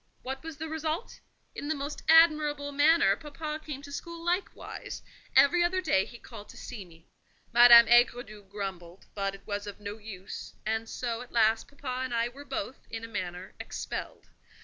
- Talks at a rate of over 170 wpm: Yes, average, 180 wpm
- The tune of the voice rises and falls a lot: Yes, wide, 6.4 semitones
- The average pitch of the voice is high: Yes, high, 245 Hz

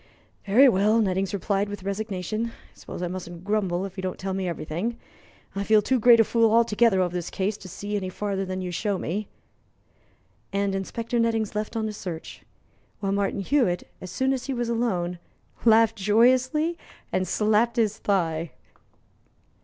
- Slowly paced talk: No, average, 175 wpm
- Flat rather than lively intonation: No, average, 3.5 semitones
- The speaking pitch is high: Yes, high, 205 Hz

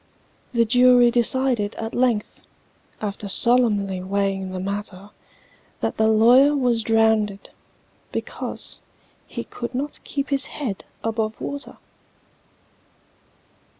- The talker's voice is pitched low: No, high, 225 Hz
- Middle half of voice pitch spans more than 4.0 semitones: No, average, 3.5 semitones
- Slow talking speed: Yes, slow, 105 wpm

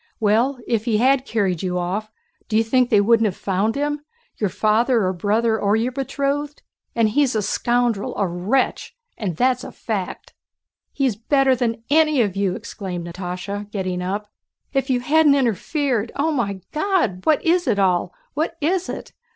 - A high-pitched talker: Yes, high, 225 Hz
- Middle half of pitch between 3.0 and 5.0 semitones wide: No, wide, 5.4 semitones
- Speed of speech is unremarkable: Yes, average, 170 wpm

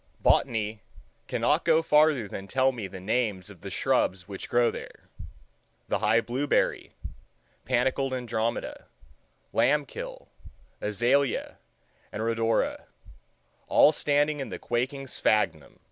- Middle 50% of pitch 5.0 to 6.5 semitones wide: No, average, 4.5 semitones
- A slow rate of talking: Yes, slow, 110 wpm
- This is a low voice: Yes, low, 120 Hz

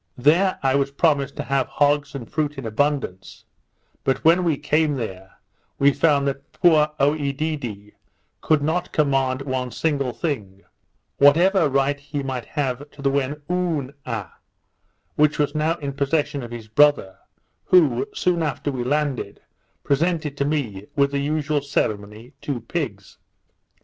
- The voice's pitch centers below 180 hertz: Yes, medium, 140 Hz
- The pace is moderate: Yes, average, 145 wpm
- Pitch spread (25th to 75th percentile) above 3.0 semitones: No, narrow, 2.6 semitones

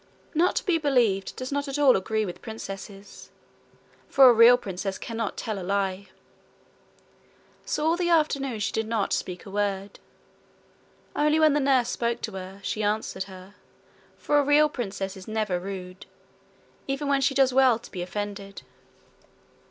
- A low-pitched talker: No, high, 220 Hz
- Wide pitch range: Yes, wide, 5.8 semitones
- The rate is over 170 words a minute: No, average, 165 wpm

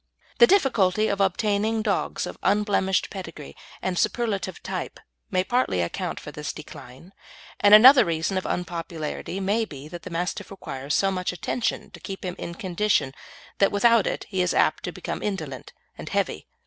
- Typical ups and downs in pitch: Yes, average, 3.6 semitones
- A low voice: No, high, 190 Hz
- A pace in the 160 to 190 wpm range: Yes, average, 170 wpm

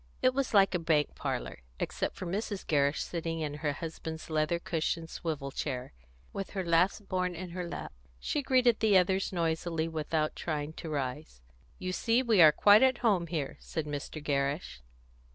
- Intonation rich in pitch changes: No, average, 3.8 semitones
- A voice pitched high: No, medium, 165 Hz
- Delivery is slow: No, average, 175 wpm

